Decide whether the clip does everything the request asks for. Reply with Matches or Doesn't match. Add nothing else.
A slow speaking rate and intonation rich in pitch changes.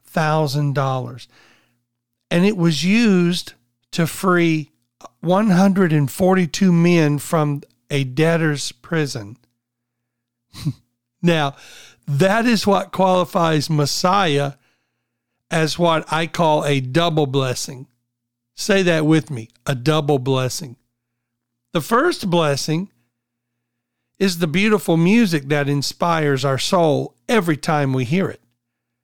Matches